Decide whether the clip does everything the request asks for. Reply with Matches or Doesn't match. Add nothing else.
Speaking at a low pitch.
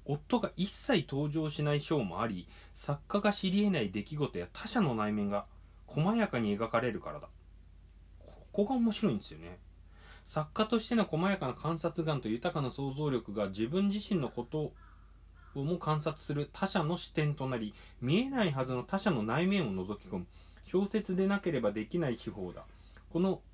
Doesn't match